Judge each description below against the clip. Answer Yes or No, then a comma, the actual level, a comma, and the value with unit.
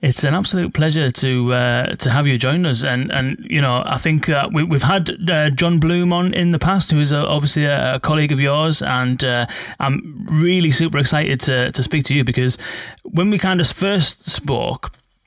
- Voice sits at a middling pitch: Yes, medium, 150 Hz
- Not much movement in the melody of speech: No, average, 4.3 semitones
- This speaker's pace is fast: Yes, fast, 215 wpm